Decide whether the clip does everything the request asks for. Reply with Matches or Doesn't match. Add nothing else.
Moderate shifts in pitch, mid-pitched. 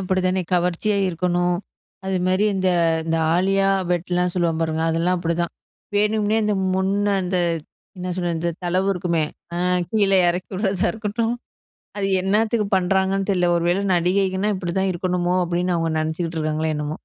Doesn't match